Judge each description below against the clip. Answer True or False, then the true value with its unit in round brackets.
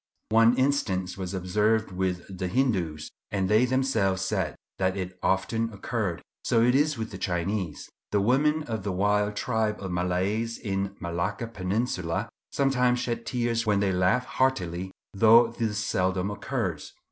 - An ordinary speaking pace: True (155 wpm)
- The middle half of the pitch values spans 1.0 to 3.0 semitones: False (3.9 semitones)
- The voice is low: True (105 Hz)